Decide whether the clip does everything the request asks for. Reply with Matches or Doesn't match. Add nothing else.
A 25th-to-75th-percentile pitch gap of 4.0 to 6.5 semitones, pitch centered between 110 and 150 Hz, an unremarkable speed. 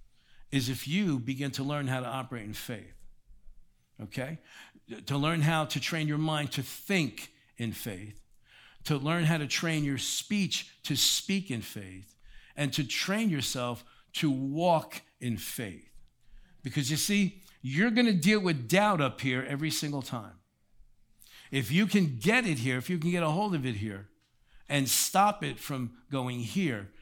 Matches